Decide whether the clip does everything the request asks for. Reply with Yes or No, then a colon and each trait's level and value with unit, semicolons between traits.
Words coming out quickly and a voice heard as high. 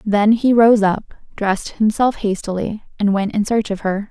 No: average, 190 wpm; high, 210 Hz